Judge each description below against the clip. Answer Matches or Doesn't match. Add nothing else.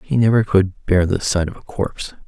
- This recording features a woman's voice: Doesn't match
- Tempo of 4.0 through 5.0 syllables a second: Doesn't match